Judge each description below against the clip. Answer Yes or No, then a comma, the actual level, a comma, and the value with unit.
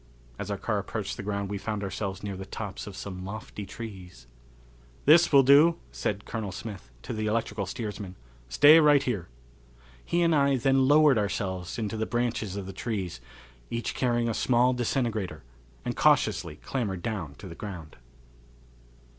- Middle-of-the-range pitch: No, low, 105 Hz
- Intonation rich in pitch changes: No, average, 4.3 semitones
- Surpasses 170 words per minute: No, average, 165 wpm